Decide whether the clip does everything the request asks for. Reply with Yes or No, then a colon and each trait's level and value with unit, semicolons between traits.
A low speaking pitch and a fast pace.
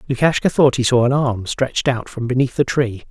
Yes: low, 130 Hz; fast, 230 wpm